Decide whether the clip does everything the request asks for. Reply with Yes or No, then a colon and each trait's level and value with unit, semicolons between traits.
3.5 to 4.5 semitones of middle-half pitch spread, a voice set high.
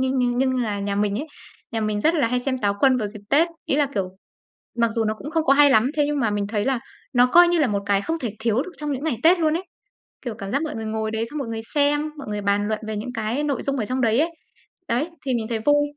No: average, 5.1 semitones; high, 245 Hz